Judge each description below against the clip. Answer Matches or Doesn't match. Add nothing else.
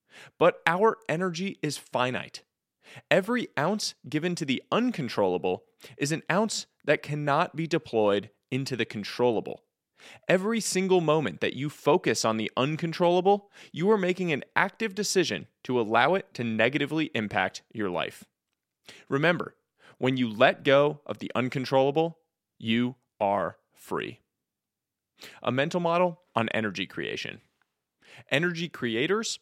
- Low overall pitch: Doesn't match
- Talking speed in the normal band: Doesn't match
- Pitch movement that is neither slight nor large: Doesn't match